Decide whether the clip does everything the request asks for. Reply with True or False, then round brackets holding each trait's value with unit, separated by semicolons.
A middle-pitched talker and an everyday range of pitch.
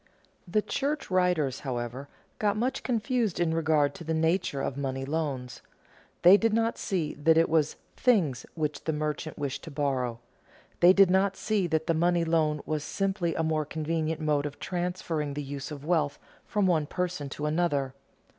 True (160 Hz; 3.7 semitones)